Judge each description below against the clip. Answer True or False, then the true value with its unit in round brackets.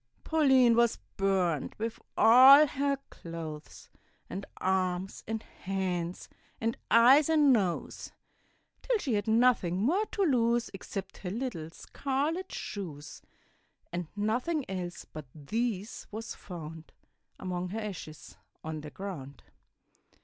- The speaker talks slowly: True (120 wpm)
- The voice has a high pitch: True (205 Hz)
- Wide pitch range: True (6.1 semitones)